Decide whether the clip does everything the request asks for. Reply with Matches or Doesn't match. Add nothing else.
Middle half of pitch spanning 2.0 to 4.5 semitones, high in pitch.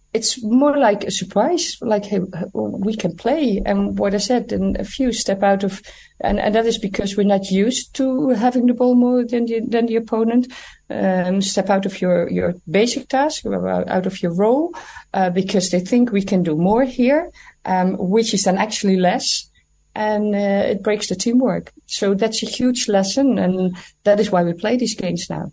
Matches